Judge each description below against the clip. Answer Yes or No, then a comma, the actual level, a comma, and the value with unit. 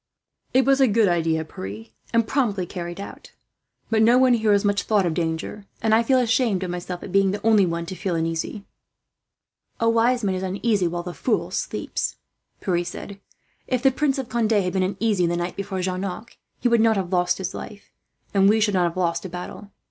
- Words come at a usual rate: No, fast, 215 wpm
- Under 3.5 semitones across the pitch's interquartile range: No, average, 4.1 semitones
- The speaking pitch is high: Yes, high, 195 Hz